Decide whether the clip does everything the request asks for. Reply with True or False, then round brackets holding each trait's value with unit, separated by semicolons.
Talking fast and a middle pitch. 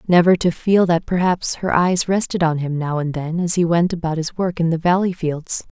True (240 wpm; 170 Hz)